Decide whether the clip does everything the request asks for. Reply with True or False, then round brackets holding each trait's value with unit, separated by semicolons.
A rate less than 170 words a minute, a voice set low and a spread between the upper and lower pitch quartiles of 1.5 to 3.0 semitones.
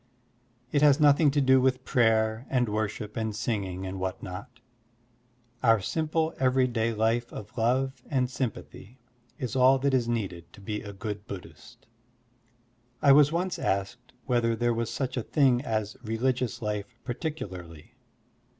False (150 wpm; 120 Hz; 3.8 semitones)